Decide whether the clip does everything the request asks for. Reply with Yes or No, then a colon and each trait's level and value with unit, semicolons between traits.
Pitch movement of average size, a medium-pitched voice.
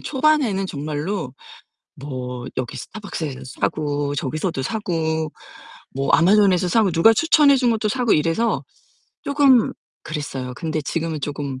No: wide, 7.2 semitones; medium, 165 Hz